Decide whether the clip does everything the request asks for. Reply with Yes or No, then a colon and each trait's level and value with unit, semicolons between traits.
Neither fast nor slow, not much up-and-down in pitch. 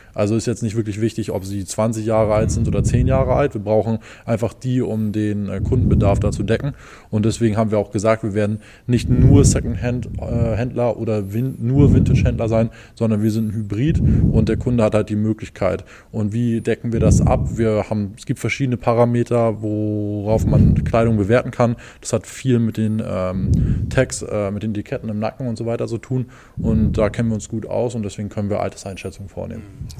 No: fast, 205 wpm; narrow, 2.0 semitones